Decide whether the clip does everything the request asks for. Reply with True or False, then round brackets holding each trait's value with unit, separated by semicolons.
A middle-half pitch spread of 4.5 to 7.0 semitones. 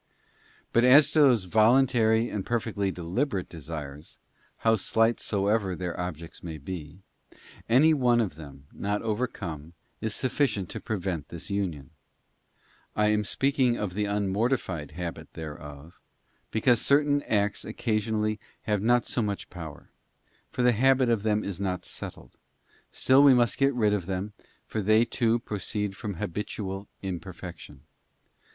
True (4.8 semitones)